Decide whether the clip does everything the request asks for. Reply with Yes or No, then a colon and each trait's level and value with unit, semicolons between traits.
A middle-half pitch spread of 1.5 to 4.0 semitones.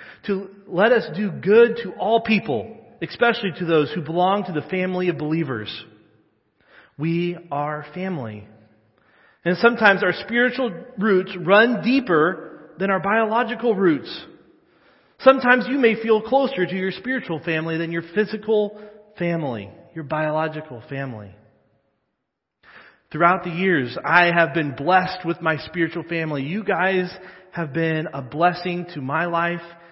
No: average, 4.6 semitones